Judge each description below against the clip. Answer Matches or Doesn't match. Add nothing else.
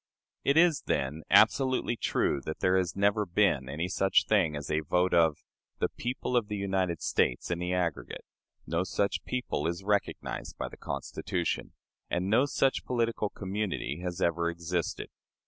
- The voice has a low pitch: Matches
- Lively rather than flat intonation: Doesn't match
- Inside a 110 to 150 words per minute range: Doesn't match